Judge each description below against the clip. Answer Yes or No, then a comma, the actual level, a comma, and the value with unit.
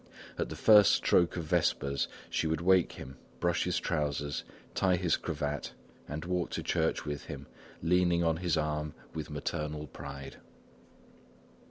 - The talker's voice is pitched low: Yes, very low, 80 Hz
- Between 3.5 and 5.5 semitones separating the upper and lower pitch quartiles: No, average, 2.9 semitones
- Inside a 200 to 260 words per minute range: No, average, 155 wpm